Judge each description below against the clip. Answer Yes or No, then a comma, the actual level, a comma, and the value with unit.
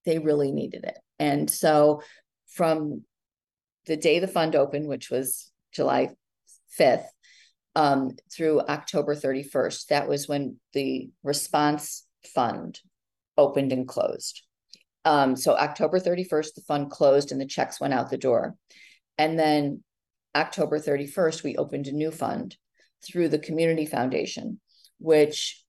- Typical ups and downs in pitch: No, narrow, 2.0 semitones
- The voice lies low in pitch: No, medium, 150 Hz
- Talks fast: No, slow, 135 wpm